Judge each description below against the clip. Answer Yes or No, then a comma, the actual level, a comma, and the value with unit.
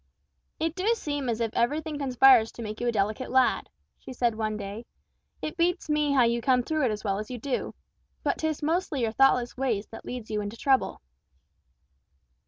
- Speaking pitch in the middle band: No, very high, 250 Hz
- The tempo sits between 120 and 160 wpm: No, average, 195 wpm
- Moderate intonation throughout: Yes, average, 4.7 semitones